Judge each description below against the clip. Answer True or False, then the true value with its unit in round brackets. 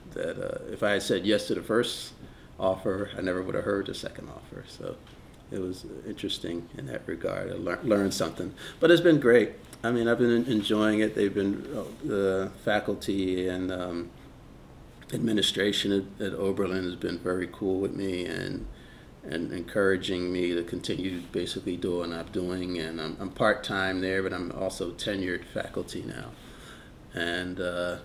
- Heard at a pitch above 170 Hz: False (95 Hz)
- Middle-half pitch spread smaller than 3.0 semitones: True (2.4 semitones)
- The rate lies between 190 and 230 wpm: False (170 wpm)